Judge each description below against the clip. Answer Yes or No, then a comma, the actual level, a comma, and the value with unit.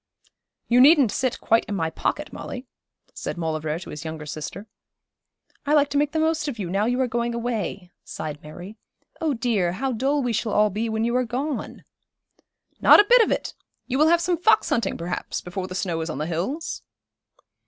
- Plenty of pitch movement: Yes, wide, 7.7 semitones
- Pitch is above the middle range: Yes, high, 230 Hz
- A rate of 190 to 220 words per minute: Yes, fast, 205 wpm